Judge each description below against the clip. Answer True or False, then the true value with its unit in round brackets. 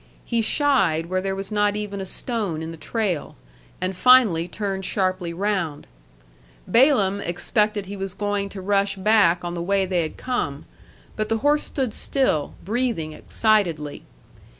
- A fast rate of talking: False (155 wpm)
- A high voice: True (195 Hz)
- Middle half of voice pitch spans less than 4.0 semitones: True (3.6 semitones)